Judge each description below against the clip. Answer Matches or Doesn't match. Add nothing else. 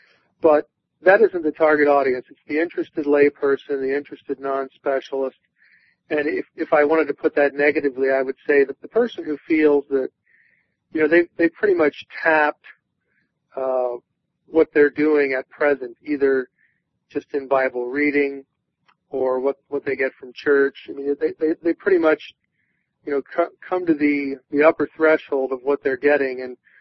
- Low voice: Doesn't match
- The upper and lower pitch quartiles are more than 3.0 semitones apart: Doesn't match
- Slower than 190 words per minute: Matches